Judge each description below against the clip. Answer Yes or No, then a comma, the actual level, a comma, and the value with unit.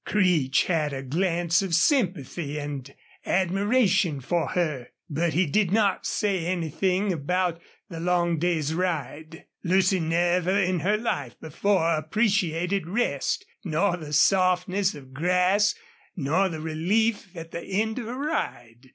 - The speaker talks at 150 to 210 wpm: No, slow, 135 wpm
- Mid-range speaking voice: Yes, medium, 175 Hz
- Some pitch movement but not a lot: Yes, average, 3.6 semitones